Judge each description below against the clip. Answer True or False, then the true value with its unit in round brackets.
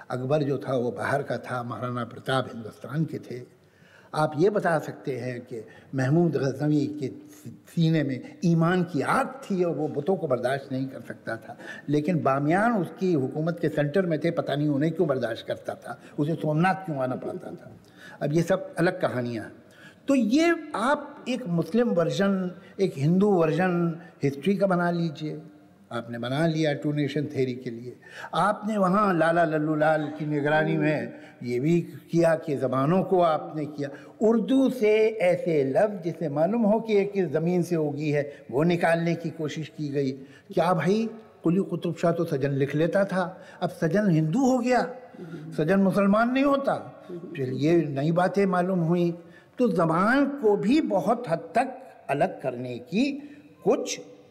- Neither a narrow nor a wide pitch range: True (4.9 semitones)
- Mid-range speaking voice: True (165 Hz)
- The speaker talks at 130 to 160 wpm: False (170 wpm)